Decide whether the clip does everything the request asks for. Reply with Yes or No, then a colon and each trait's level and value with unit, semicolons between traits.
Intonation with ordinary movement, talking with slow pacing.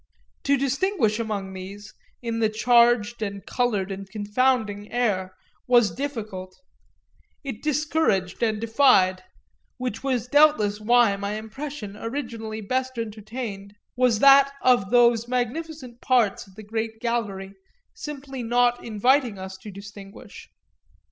Yes: average, 3.7 semitones; slow, 120 wpm